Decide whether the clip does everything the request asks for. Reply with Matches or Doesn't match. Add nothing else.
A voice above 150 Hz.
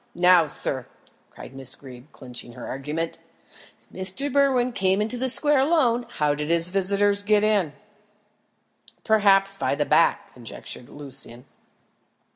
Matches